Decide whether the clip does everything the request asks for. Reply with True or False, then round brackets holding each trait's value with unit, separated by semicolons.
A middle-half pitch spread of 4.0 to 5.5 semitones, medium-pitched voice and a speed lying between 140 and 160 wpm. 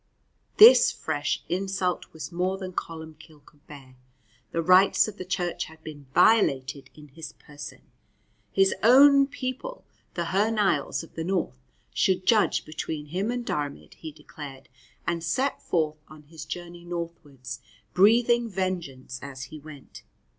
True (4.5 semitones; 170 Hz; 145 wpm)